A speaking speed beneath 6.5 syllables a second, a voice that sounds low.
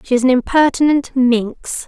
No: 4.5 syllables/s; very high, 260 Hz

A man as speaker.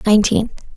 No: female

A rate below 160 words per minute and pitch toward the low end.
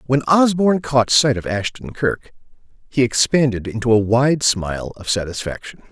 Yes: average, 150 wpm; low, 125 Hz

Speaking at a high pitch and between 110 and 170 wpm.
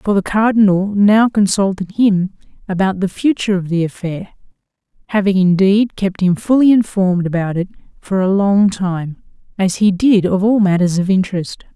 Yes: high, 195 Hz; average, 165 wpm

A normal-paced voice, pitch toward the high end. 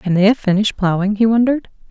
No: fast, 220 wpm; high, 210 Hz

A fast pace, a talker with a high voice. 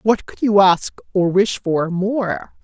No: average, 180 wpm; high, 195 Hz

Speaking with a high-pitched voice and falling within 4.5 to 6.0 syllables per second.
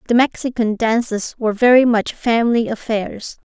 Yes: high, 230 Hz; 5.0 syllables/s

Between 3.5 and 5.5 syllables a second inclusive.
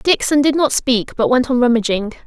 Yes: 5.2 syllables/s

